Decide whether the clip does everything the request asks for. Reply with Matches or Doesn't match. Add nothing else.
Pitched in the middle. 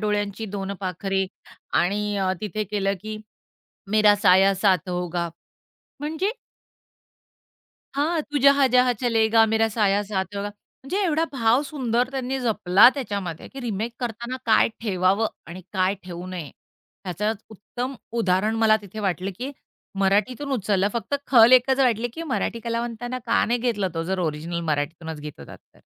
Doesn't match